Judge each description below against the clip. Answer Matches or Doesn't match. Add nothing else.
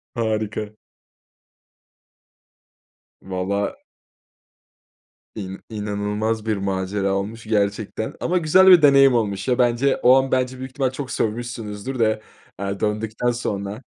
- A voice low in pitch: Matches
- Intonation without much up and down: Doesn't match